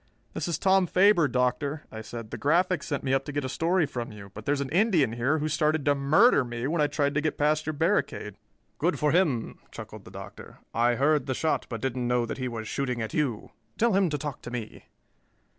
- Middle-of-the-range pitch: Yes, medium, 145 Hz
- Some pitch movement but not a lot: Yes, average, 4.4 semitones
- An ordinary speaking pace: No, fast, 235 wpm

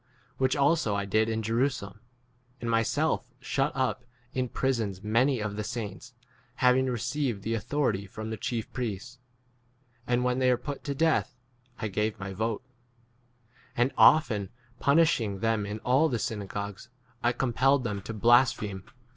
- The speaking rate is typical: Yes, average, 160 wpm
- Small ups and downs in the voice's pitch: No, average, 3.7 semitones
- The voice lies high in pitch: No, low, 120 Hz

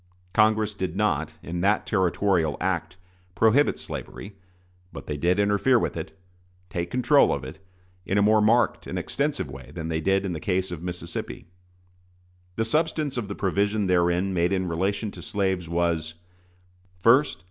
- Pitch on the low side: Yes, very low, 95 Hz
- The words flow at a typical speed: Yes, average, 160 wpm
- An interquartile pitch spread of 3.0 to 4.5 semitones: Yes, average, 3.7 semitones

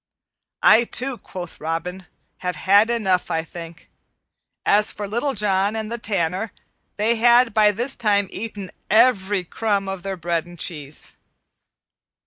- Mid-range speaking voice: No, high, 200 Hz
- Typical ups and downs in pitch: Yes, average, 3.8 semitones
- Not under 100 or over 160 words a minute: Yes, average, 140 wpm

